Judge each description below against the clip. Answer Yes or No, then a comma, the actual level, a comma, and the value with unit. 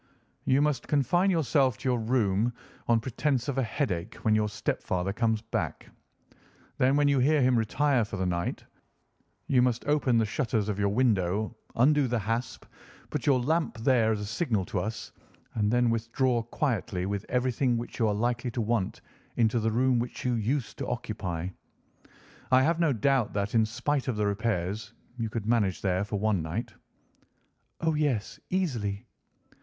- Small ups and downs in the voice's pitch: No, average, 3.8 semitones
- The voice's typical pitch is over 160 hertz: No, low, 115 Hz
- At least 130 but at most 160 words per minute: No, average, 175 wpm